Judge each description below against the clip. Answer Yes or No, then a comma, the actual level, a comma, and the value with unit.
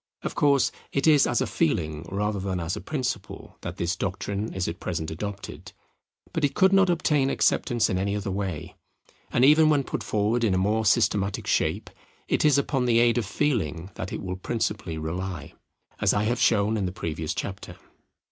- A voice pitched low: Yes, low, 100 Hz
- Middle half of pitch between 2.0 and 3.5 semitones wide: No, average, 5.1 semitones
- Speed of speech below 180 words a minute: No, average, 195 wpm